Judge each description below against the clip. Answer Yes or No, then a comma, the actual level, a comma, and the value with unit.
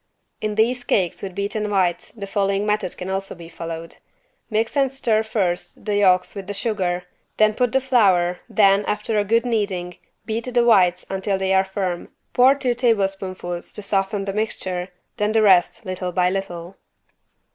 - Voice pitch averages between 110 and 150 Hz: No, high, 195 Hz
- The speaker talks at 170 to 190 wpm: Yes, average, 175 wpm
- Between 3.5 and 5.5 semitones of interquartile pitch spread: No, average, 3.0 semitones